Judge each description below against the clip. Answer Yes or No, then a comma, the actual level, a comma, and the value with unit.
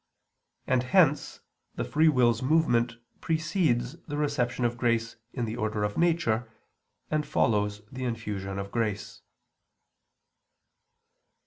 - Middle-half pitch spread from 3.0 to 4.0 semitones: No, average, 5.1 semitones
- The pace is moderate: No, slow, 115 wpm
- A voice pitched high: No, low, 120 Hz